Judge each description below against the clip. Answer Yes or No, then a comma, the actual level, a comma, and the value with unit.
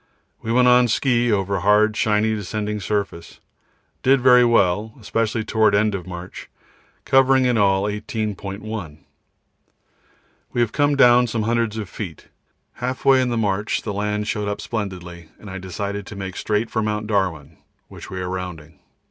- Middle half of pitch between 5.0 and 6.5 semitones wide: No, average, 3.0 semitones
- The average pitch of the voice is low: Yes, low, 105 Hz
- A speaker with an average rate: Yes, average, 165 wpm